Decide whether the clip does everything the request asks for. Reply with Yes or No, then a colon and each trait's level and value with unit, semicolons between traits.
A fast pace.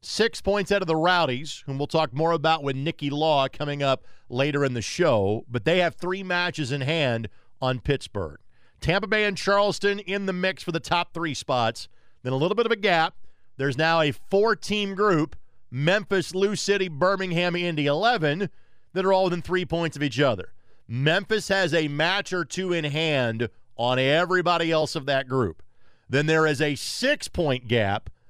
No: average, 190 wpm